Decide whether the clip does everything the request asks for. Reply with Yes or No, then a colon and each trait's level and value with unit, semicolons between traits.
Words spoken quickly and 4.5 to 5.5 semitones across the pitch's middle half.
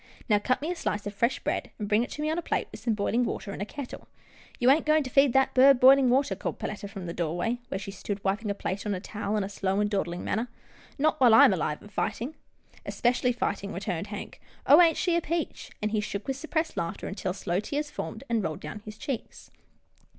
Yes: fast, 265 wpm; average, 5.1 semitones